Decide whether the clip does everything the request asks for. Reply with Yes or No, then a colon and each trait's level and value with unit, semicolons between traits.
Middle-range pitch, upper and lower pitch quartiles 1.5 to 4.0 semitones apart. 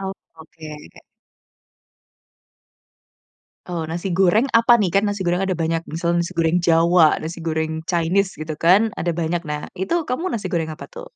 Yes: medium, 175 Hz; average, 3.0 semitones